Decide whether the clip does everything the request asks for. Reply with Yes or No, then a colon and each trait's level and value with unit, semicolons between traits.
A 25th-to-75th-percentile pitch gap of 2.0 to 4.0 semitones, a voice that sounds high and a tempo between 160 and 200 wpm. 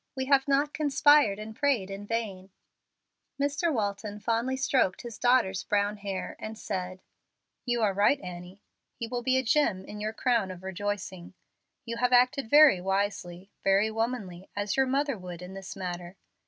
No: average, 4.9 semitones; high, 210 Hz; average, 170 wpm